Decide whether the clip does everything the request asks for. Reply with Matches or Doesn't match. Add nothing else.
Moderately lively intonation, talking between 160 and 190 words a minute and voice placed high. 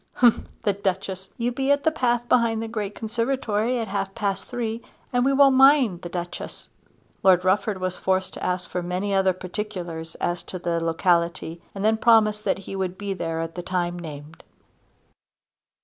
Matches